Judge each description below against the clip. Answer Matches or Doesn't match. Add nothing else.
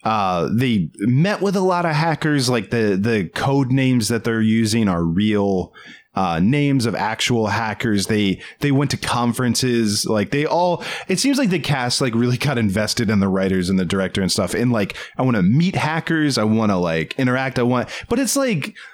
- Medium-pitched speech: Doesn't match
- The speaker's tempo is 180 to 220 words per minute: Matches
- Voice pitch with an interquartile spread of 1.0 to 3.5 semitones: Doesn't match